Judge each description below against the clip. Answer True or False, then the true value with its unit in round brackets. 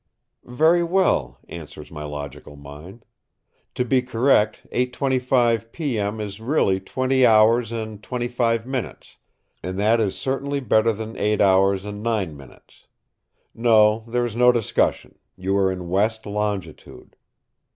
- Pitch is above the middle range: False (110 Hz)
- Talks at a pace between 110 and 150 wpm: True (135 wpm)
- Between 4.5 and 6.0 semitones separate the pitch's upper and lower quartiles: False (4.1 semitones)